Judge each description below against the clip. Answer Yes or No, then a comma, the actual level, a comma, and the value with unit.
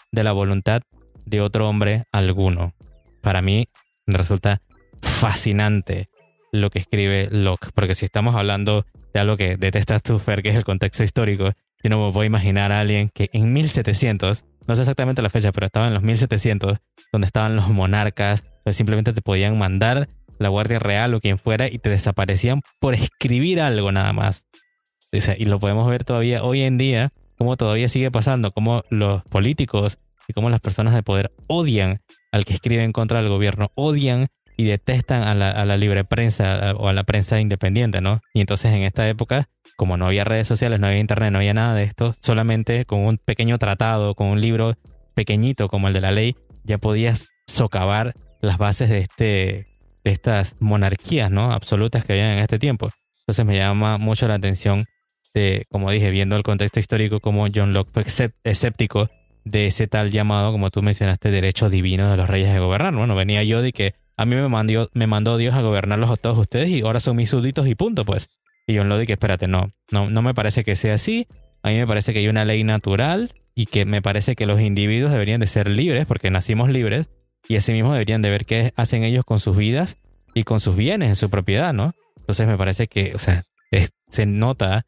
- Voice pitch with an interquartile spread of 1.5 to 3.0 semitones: Yes, narrow, 2.5 semitones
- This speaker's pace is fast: Yes, fast, 205 wpm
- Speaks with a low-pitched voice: Yes, low, 105 Hz